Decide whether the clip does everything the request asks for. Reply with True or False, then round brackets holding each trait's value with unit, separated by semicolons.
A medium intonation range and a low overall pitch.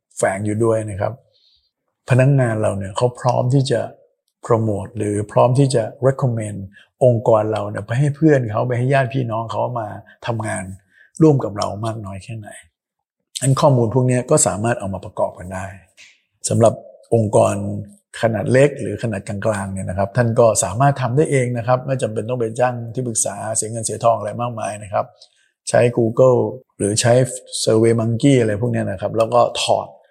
True (3.2 semitones; 115 Hz)